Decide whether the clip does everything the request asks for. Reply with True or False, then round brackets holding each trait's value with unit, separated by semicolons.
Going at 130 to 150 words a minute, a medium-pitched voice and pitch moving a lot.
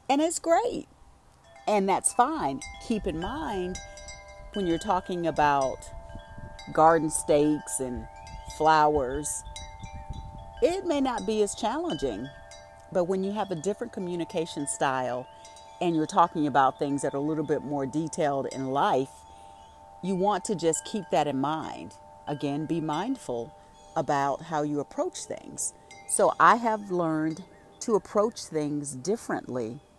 True (140 wpm; 155 Hz; 7.1 semitones)